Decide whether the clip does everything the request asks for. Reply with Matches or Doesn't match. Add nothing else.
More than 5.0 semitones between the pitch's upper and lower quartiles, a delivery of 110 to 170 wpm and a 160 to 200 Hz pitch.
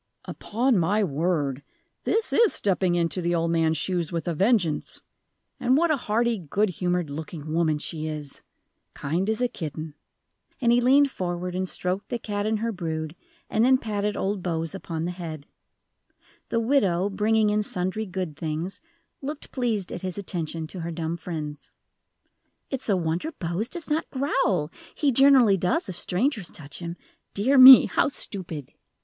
Matches